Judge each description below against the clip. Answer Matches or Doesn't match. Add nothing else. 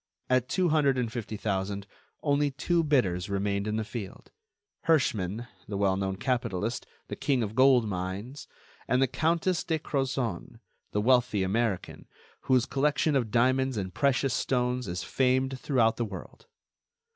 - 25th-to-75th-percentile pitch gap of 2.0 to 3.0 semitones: Doesn't match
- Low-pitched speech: Matches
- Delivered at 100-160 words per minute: Matches